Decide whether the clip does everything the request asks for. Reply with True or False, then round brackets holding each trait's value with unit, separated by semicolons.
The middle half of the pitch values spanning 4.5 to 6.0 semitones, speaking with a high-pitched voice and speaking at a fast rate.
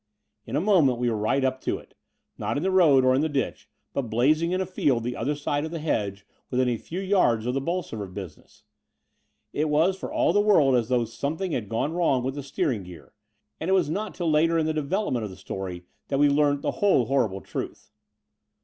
False (5.5 semitones; 140 Hz; 240 wpm)